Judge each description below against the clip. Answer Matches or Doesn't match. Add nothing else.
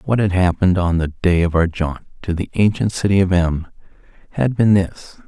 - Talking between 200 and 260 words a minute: Matches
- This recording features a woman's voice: Doesn't match